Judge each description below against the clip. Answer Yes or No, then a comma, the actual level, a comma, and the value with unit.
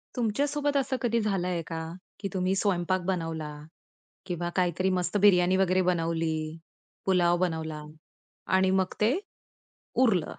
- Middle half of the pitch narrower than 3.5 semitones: Yes, narrow, 2.6 semitones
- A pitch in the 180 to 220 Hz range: Yes, medium, 185 Hz